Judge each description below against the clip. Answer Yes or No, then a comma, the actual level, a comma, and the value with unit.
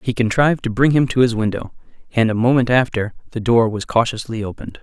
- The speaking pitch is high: No, low, 120 Hz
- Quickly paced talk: Yes, fast, 210 wpm